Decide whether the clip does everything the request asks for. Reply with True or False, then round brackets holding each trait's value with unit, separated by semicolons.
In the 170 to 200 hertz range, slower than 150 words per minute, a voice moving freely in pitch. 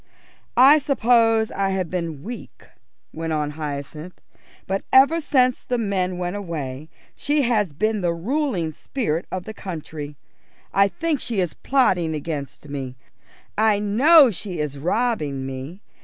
True (185 Hz; 140 wpm; 7.1 semitones)